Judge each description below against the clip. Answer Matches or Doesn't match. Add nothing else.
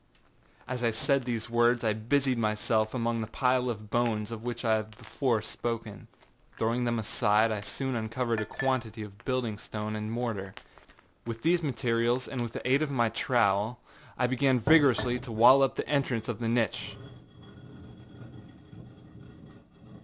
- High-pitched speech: Doesn't match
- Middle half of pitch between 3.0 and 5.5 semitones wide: Doesn't match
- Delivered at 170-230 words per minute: Doesn't match